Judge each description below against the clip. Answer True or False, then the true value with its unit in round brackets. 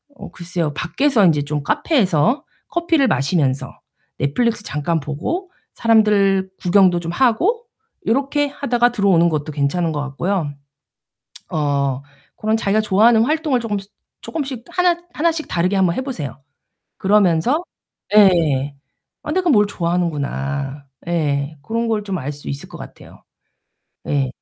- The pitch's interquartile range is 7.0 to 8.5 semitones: True (8.0 semitones)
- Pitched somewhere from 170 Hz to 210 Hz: True (190 Hz)